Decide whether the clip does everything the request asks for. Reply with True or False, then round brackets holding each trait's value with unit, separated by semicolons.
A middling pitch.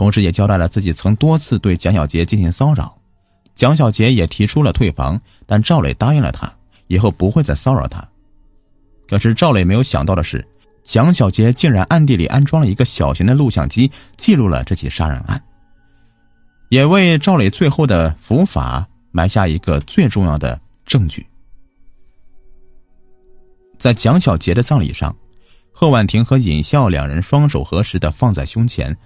False (105 Hz)